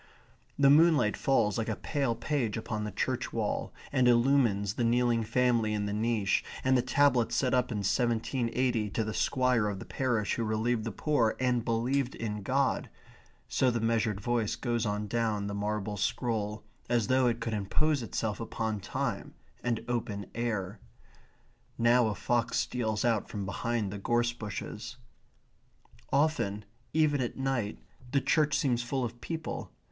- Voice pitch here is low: Yes, low, 115 Hz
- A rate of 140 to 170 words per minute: Yes, average, 165 wpm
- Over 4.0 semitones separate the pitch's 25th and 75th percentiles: No, average, 3.0 semitones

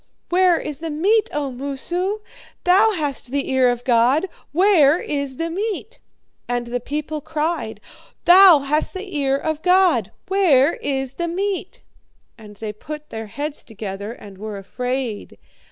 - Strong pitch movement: Yes, wide, 6.2 semitones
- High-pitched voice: Yes, very high, 295 Hz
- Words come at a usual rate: Yes, average, 150 wpm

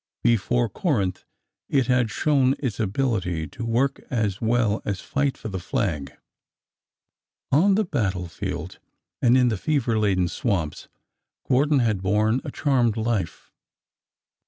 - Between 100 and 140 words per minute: Yes, slow, 135 wpm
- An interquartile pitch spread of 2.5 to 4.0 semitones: No, average, 4.9 semitones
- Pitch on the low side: Yes, low, 115 Hz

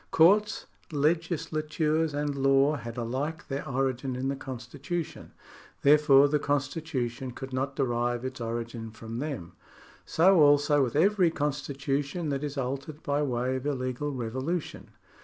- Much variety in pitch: No, average, 2.8 semitones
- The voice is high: No, medium, 140 Hz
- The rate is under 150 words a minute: Yes, average, 140 wpm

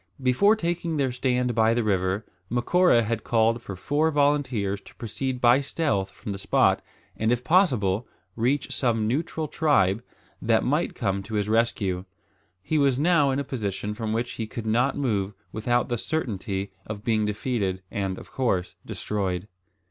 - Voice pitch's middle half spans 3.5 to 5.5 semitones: Yes, average, 4.7 semitones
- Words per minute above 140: Yes, average, 165 wpm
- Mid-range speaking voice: No, low, 115 Hz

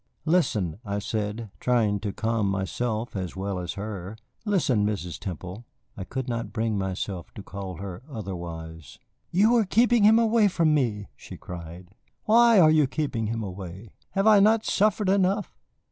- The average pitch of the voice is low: Yes, low, 110 Hz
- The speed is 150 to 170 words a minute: Yes, average, 160 wpm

